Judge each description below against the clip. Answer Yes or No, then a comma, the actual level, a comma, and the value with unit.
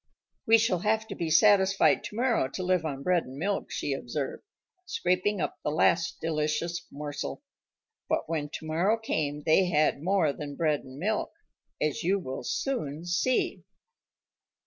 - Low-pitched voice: No, medium, 170 Hz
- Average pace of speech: Yes, average, 150 wpm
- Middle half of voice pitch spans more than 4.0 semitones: Yes, average, 4.9 semitones